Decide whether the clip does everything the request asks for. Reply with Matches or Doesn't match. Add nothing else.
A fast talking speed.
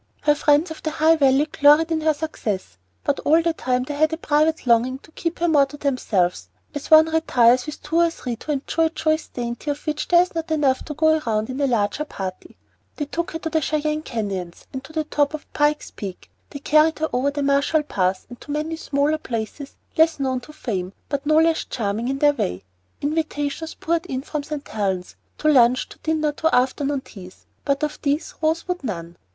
Matches